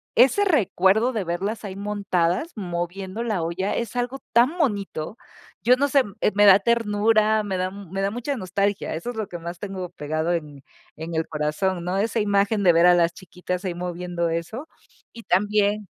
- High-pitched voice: Yes, high, 195 Hz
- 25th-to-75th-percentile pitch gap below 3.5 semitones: No, average, 3.8 semitones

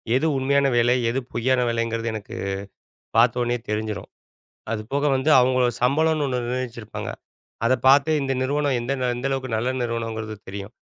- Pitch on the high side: No, low, 125 Hz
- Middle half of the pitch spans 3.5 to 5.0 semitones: No, average, 2.7 semitones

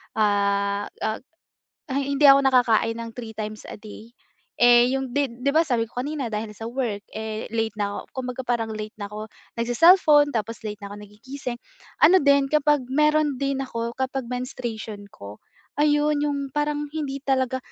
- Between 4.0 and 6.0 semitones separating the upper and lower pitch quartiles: Yes, average, 4.3 semitones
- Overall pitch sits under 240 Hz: No, high, 245 Hz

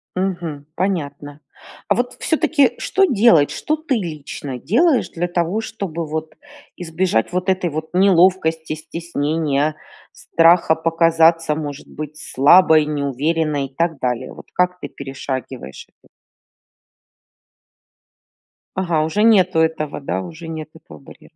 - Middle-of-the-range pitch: Yes, medium, 165 Hz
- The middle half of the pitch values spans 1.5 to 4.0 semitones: Yes, average, 3.5 semitones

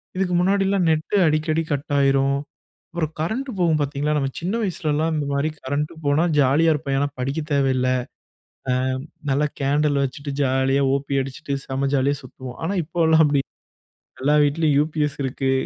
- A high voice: No, medium, 145 Hz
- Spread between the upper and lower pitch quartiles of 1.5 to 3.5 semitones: Yes, narrow, 2.6 semitones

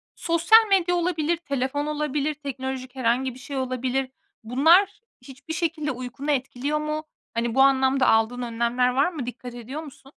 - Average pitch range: Yes, average, 3.3 semitones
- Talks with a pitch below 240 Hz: No, very high, 270 Hz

